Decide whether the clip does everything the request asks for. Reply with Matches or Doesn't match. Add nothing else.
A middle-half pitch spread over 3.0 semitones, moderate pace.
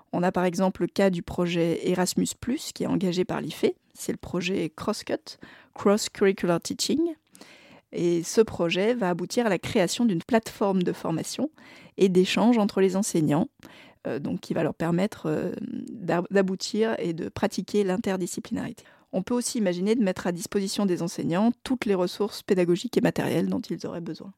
Matches